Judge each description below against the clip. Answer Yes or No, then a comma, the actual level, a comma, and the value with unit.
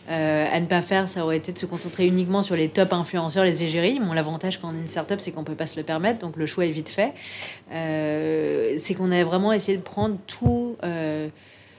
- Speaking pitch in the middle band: Yes, medium, 170 Hz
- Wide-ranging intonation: No, average, 3.0 semitones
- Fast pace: Yes, fast, 245 wpm